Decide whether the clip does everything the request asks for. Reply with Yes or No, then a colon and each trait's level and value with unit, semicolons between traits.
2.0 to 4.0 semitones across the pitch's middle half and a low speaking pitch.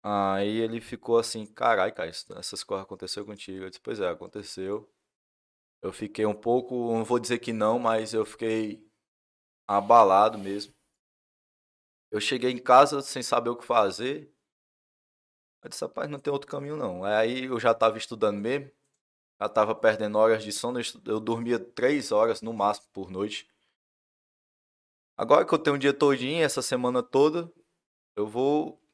Yes: average, 3.2 semitones; low, 115 Hz